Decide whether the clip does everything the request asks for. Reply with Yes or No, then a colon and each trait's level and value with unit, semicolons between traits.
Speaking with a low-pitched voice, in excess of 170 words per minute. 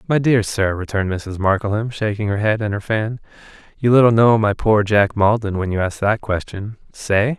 Yes: low, 105 Hz; fast, 205 wpm